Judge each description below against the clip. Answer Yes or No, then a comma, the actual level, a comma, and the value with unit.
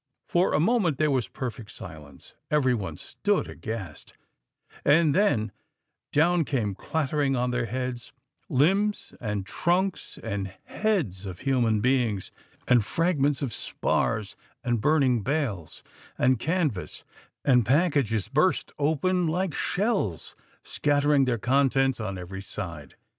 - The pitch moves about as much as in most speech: No, wide, 6.4 semitones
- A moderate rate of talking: No, slow, 125 wpm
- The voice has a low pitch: Yes, low, 130 Hz